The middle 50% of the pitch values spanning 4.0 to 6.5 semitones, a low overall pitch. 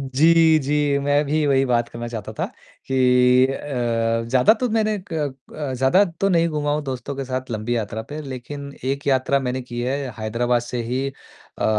No: average, 3.2 semitones; low, 130 Hz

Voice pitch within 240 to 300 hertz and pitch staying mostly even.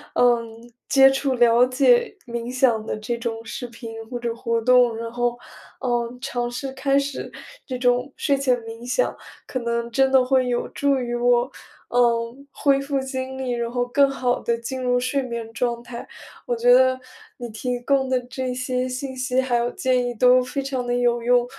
Yes: high, 245 Hz; narrow, 1.6 semitones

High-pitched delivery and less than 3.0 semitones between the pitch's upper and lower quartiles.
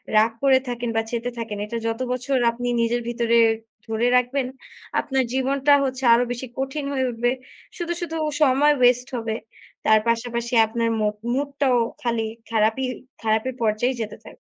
Yes: high, 245 Hz; narrow, 2.5 semitones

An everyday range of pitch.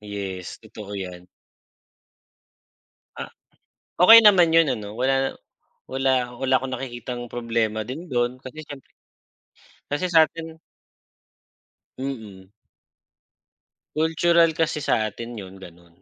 No: wide, 6.5 semitones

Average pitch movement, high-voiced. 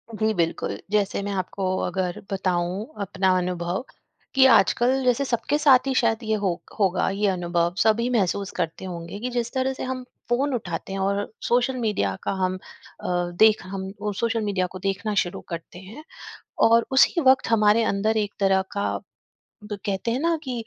Yes: average, 4.2 semitones; high, 205 Hz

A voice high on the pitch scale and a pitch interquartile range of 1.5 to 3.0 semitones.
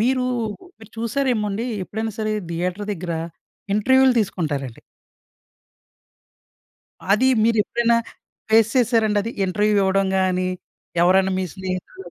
No: high, 210 Hz; average, 3.4 semitones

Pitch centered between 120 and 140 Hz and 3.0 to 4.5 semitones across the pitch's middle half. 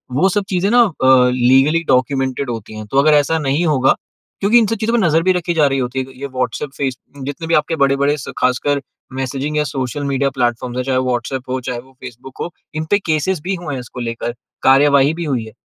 Yes: low, 135 Hz; average, 3.4 semitones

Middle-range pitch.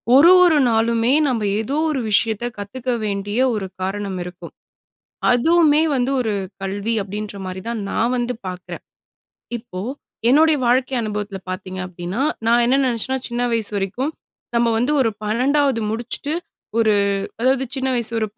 No: high, 230 Hz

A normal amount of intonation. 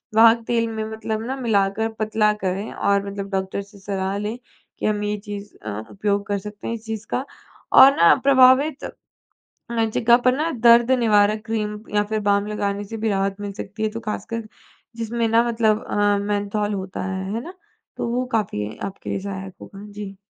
No: narrow, 2.2 semitones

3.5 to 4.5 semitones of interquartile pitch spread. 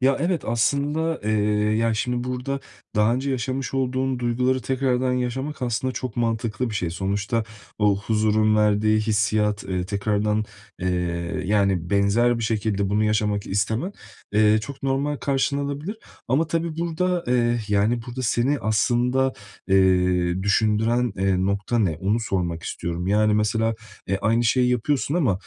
Yes: average, 3.9 semitones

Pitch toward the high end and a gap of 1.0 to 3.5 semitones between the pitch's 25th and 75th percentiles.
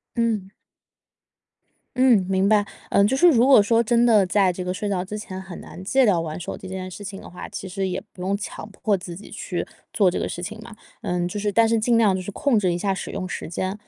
Yes: high, 200 Hz; average, 2.8 semitones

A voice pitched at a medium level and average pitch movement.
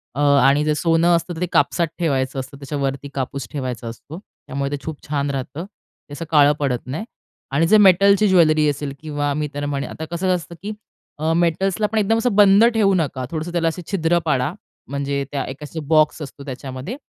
Yes: medium, 150 Hz; average, 3.8 semitones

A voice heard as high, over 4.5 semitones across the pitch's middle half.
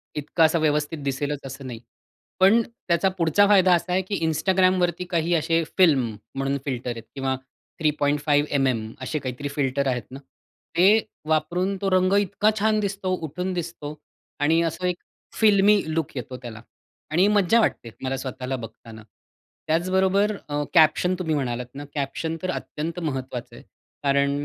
No: medium, 155 Hz; average, 5.2 semitones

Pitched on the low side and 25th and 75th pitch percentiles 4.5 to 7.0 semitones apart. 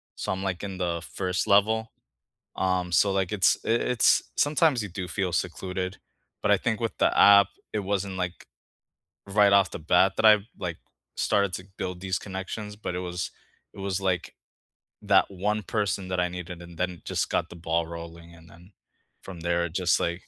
No: very low, 95 Hz; narrow, 2.4 semitones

